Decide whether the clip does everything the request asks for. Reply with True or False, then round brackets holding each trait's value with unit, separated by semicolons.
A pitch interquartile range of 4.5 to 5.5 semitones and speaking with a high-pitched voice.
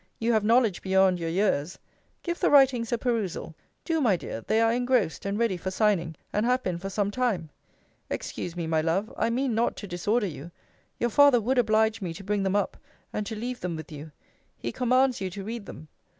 True (4.8 semitones; 210 Hz)